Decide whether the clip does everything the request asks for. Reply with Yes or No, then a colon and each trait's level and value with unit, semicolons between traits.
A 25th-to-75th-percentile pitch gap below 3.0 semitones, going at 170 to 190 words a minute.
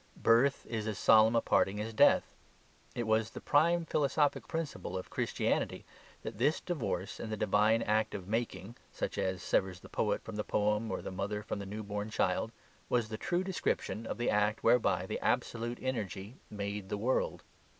Yes: narrow, 2.6 semitones; average, 185 wpm